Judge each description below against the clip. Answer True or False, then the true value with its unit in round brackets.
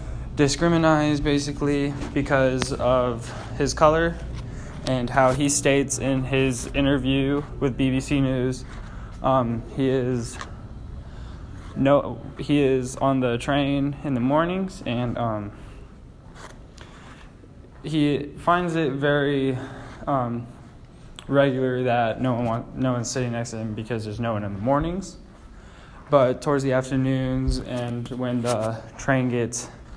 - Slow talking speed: True (125 wpm)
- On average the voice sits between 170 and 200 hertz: False (130 Hz)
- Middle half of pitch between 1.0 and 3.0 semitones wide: True (2.7 semitones)